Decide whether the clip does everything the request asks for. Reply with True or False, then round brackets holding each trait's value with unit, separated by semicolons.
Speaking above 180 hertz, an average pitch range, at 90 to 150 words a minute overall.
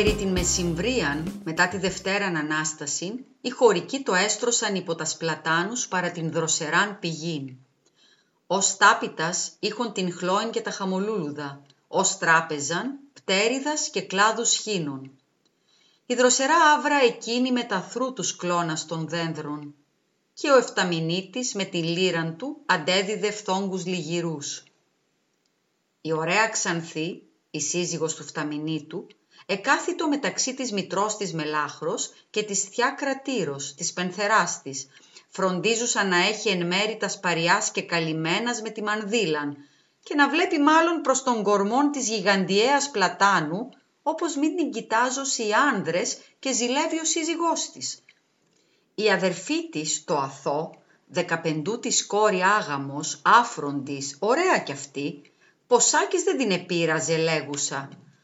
False (190 Hz; 6.7 semitones; 125 wpm)